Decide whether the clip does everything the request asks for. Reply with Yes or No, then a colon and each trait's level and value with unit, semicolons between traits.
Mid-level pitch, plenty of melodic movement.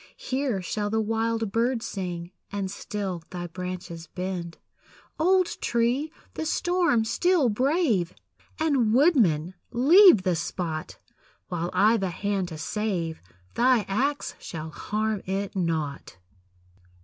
No: high, 205 Hz; wide, 5.9 semitones